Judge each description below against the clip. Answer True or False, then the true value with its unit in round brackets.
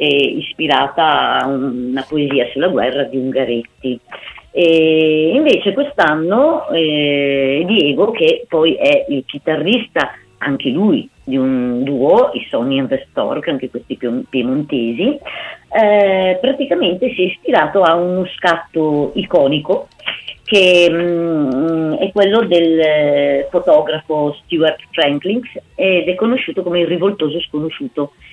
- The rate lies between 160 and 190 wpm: False (120 wpm)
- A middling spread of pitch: False (6.0 semitones)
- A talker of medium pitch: True (165 Hz)